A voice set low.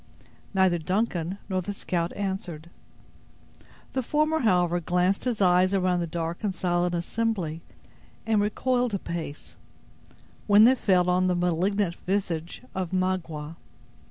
No: medium, 185 Hz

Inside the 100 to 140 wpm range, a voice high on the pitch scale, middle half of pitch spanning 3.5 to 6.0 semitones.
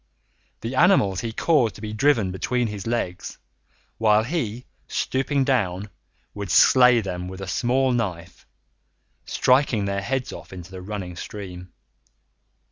No: slow, 135 wpm; low, 105 Hz; average, 4.9 semitones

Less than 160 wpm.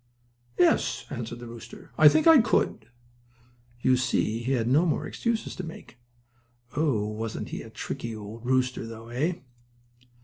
Yes: average, 150 wpm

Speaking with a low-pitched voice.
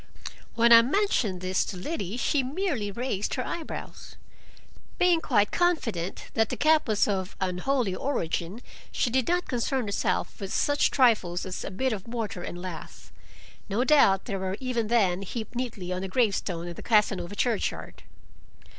No: high, 220 Hz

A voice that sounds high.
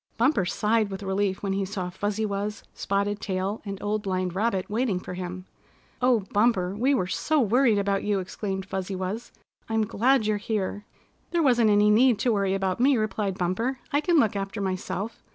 Yes: high, 205 Hz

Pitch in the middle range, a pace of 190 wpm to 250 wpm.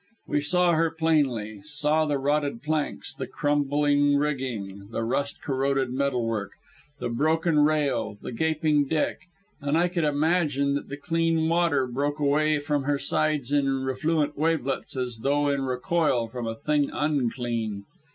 No: medium, 145 Hz; average, 150 wpm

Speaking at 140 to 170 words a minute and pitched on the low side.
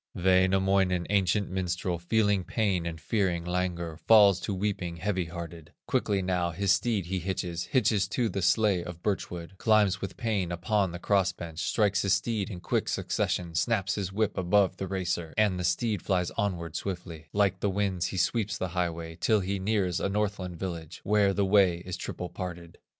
No: average, 185 wpm; very low, 95 Hz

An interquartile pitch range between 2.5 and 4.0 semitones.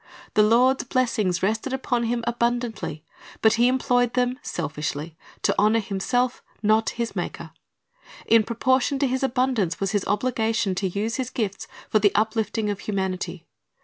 Yes: average, 3.5 semitones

